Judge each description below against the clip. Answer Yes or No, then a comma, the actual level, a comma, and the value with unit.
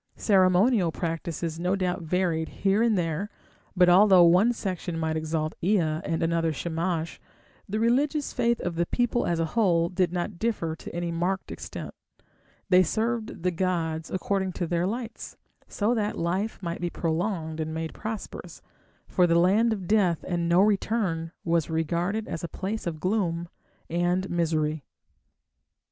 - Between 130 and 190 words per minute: Yes, average, 155 wpm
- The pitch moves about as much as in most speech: Yes, average, 3.4 semitones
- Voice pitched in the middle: Yes, medium, 175 Hz